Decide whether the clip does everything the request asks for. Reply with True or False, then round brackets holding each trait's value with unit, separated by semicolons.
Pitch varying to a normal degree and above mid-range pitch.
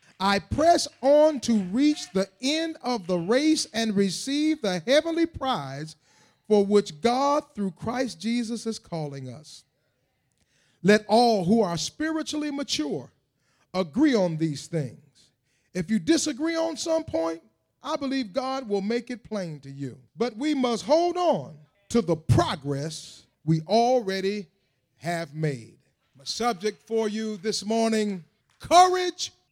False (8.9 semitones; 215 Hz)